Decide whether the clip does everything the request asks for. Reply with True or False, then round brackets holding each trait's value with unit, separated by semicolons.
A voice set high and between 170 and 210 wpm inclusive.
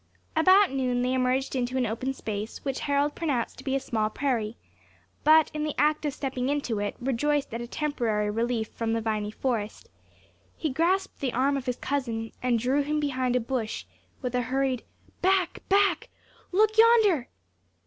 True (260 Hz; 180 wpm)